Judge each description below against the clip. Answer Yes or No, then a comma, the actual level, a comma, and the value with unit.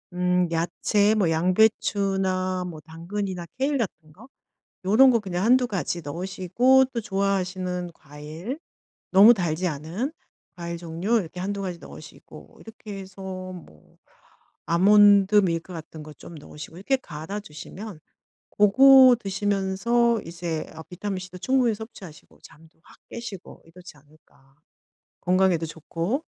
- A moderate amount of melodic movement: Yes, average, 3.7 semitones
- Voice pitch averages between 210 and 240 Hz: No, medium, 185 Hz